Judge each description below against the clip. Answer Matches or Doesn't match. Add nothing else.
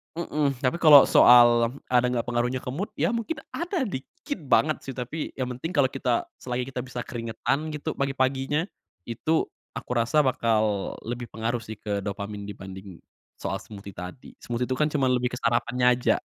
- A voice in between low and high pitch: Doesn't match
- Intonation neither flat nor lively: Matches